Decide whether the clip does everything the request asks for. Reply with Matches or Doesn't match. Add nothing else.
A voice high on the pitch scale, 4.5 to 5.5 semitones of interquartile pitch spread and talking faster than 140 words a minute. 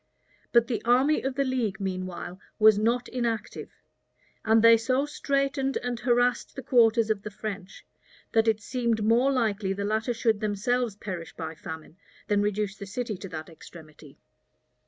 Doesn't match